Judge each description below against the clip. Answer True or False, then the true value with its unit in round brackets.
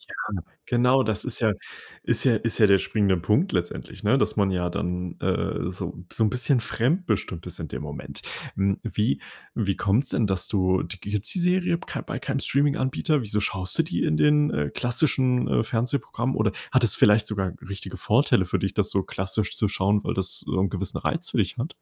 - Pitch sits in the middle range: False (105 Hz)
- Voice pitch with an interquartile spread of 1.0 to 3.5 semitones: False (4.9 semitones)